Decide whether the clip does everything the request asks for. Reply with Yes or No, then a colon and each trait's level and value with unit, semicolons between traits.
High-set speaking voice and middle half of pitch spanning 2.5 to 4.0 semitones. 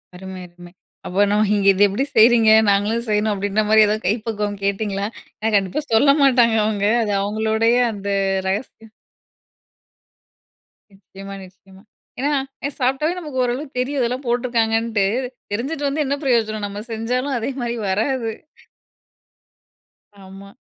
Yes: high, 220 Hz; average, 3.5 semitones